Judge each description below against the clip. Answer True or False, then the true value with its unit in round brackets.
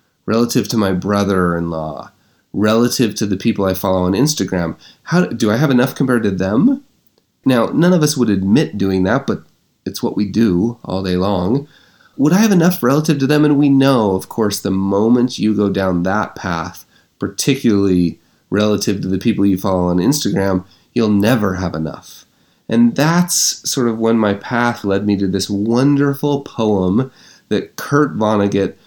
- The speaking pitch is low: True (105 Hz)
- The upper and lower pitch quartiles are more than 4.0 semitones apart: True (5.1 semitones)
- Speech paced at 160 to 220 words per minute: True (175 wpm)